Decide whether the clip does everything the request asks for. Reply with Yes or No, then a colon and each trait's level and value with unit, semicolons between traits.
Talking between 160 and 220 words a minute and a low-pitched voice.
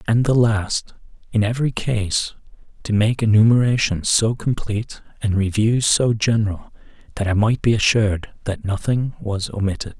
No: average, 145 wpm; low, 110 Hz